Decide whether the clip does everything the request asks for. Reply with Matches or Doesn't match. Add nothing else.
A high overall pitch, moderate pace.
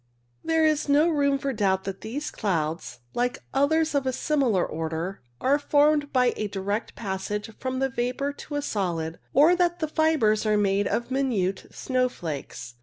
Matches